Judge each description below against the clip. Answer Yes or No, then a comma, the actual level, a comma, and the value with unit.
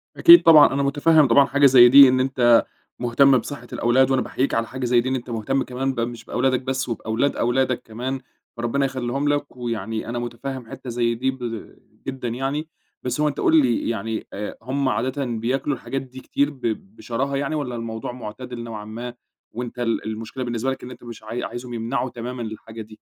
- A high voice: No, low, 125 Hz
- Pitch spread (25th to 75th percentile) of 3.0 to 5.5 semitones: No, narrow, 2.4 semitones